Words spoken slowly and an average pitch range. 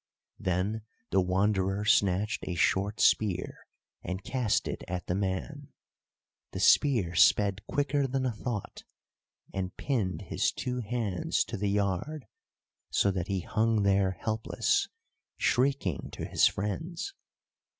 Yes: slow, 130 wpm; average, 4.6 semitones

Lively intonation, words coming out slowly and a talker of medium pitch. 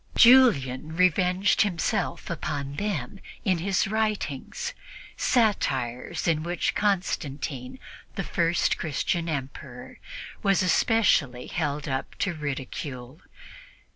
Yes: wide, 6.0 semitones; slow, 95 wpm; medium, 165 Hz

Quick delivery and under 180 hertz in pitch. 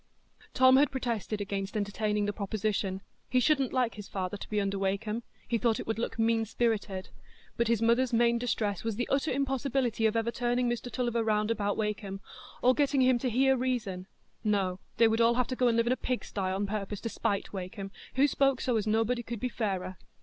No: fast, 210 wpm; high, 225 Hz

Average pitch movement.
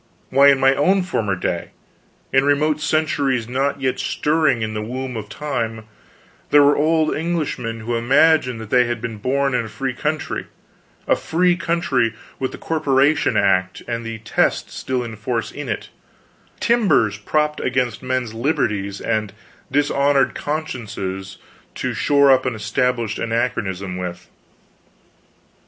Yes: average, 4.6 semitones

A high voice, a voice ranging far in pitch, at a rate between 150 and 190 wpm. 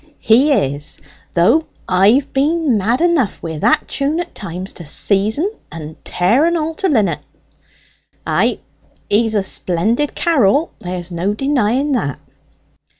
No: high, 225 Hz; wide, 8.2 semitones; average, 140 wpm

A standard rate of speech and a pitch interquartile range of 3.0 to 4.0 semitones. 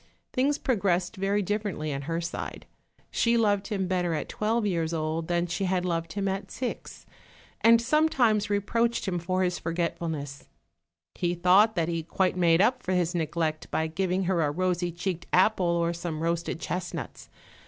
Yes: average, 170 wpm; average, 3.3 semitones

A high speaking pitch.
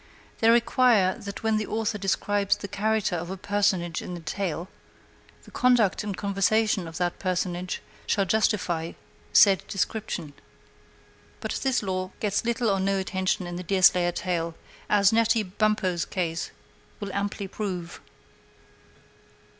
Yes: high, 195 Hz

